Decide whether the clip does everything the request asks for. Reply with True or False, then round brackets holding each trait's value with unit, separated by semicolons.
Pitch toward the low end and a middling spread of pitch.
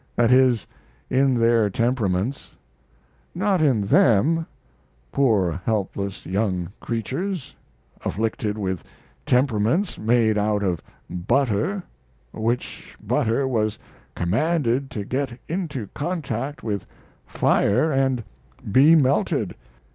True (120 Hz; 4.9 semitones)